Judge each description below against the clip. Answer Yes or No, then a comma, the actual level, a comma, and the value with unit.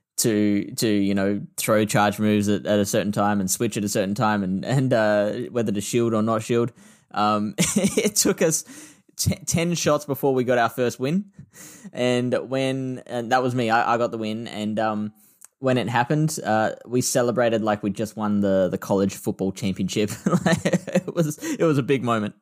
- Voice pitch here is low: Yes, low, 115 Hz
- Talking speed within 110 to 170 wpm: No, average, 200 wpm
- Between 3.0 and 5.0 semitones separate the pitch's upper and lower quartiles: Yes, average, 4.2 semitones